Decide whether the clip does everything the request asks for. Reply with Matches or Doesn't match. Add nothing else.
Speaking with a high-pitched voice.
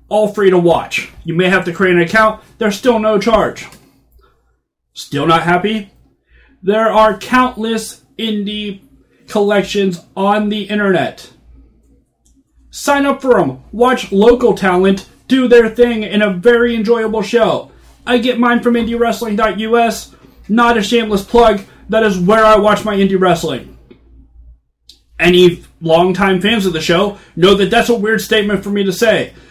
Matches